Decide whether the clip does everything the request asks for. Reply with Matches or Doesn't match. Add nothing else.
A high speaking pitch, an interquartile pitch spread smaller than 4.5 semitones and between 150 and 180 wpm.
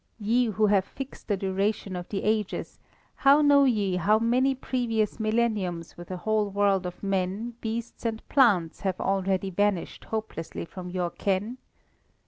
Matches